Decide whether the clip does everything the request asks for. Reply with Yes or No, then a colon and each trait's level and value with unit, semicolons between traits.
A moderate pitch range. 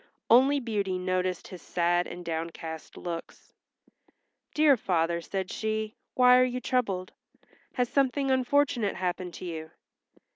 No: wide, 6.2 semitones